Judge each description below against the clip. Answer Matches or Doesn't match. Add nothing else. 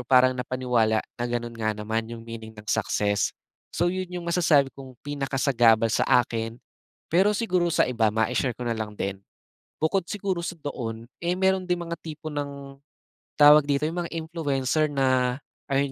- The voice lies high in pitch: Doesn't match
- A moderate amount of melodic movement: Doesn't match